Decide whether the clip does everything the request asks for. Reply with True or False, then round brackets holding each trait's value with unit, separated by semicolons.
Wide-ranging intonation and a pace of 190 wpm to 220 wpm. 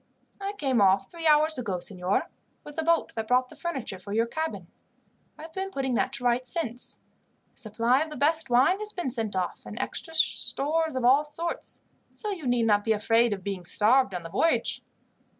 True (6.6 semitones; 205 wpm)